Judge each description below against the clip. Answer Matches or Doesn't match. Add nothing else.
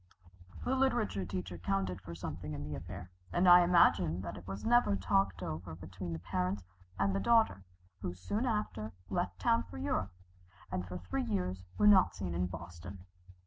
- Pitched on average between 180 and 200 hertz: Doesn't match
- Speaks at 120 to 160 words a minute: Doesn't match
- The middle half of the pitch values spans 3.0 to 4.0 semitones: Matches